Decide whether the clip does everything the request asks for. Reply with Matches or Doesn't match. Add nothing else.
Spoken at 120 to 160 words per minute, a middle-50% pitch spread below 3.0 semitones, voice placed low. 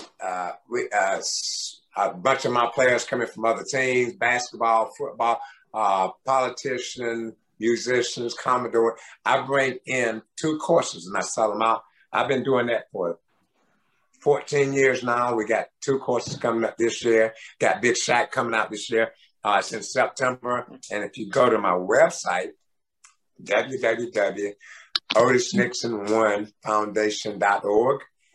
Matches